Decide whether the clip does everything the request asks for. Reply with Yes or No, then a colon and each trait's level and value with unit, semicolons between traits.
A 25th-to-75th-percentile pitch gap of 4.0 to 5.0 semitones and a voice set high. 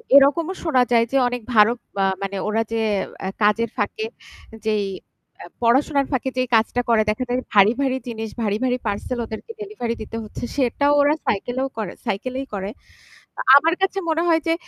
Yes: average, 4.3 semitones; high, 245 Hz